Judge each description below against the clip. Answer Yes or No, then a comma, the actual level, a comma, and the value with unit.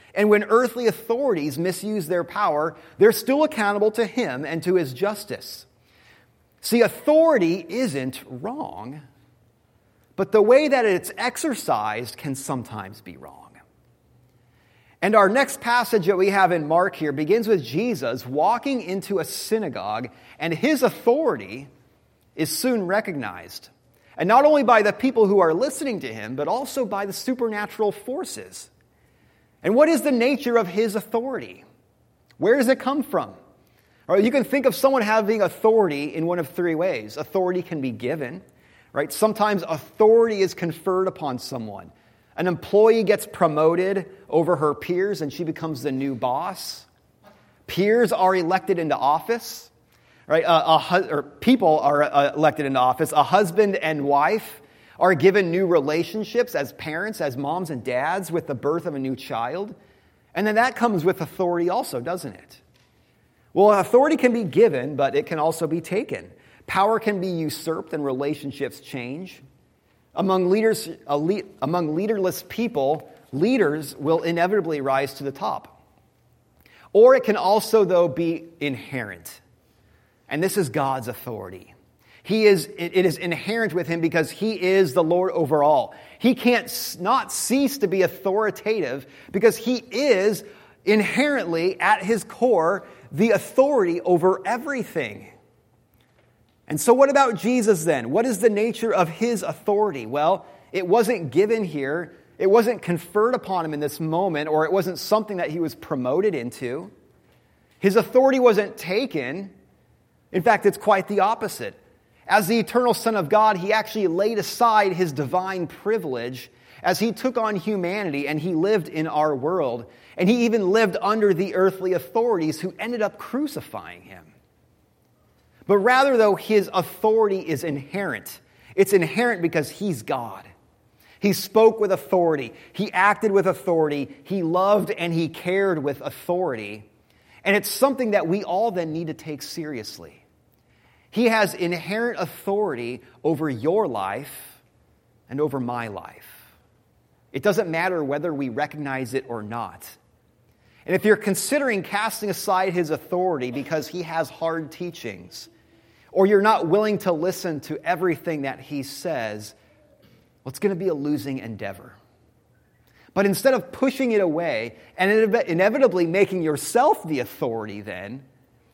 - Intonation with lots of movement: Yes, wide, 6.4 semitones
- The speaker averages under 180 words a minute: Yes, average, 150 wpm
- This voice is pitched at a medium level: Yes, medium, 180 Hz